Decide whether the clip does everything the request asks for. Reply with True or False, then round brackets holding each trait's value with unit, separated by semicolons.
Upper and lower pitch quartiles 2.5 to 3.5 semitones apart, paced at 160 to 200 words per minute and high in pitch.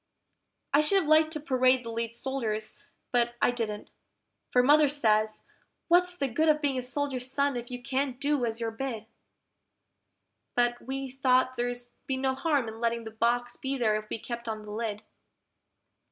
True (3.1 semitones; 180 wpm; 250 Hz)